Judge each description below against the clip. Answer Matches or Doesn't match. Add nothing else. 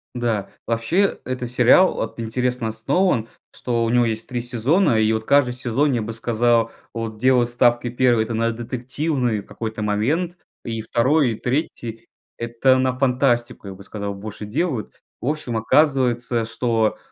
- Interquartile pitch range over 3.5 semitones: Doesn't match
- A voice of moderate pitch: Doesn't match